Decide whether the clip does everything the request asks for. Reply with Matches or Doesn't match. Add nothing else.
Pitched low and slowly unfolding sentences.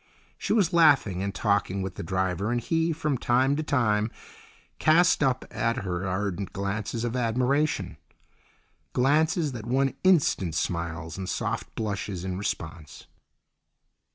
Matches